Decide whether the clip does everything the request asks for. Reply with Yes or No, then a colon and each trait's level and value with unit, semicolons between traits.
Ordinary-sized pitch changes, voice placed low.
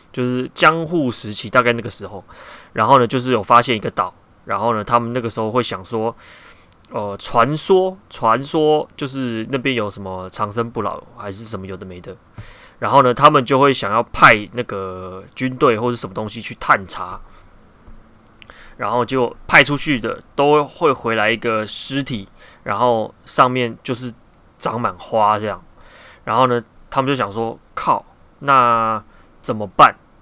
Yes: average, 3.5 semitones; low, 120 Hz